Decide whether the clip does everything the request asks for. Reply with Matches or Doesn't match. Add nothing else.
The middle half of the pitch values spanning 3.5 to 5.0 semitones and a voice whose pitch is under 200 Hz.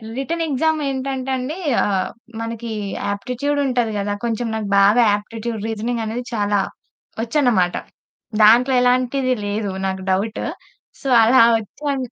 Doesn't match